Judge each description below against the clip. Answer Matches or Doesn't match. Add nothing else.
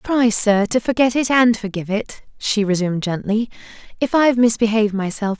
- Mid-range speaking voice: Doesn't match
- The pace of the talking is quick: Doesn't match